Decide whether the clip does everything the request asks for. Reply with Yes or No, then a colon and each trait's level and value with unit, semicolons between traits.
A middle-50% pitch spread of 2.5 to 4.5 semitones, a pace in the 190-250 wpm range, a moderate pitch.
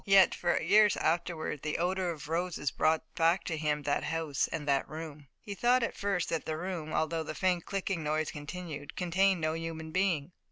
Yes: average, 2.8 semitones; average, 195 wpm; medium, 165 Hz